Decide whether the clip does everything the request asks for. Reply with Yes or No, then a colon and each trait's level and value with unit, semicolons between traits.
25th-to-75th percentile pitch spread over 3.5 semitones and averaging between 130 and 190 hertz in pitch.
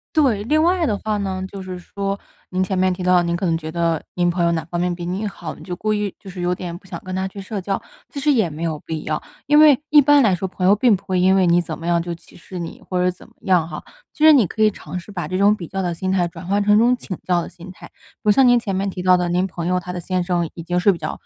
No: average, 2.7 semitones; medium, 185 Hz